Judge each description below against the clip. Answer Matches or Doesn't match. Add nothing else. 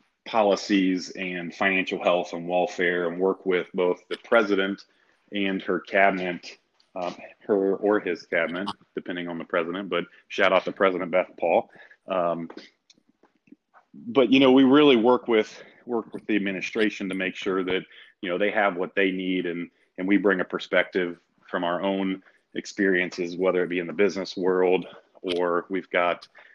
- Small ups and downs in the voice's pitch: Matches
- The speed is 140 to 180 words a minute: Matches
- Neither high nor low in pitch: Doesn't match